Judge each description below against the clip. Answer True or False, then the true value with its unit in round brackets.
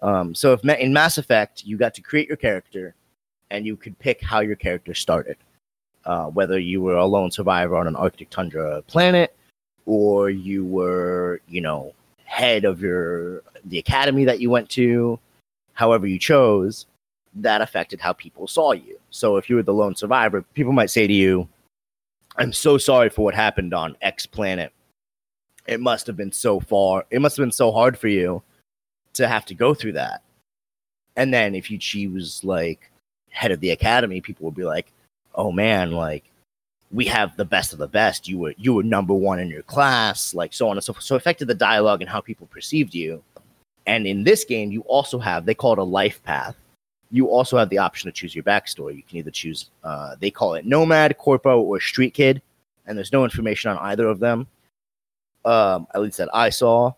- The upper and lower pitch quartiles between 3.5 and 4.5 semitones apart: False (5.6 semitones)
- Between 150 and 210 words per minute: True (205 wpm)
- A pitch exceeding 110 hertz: False (105 Hz)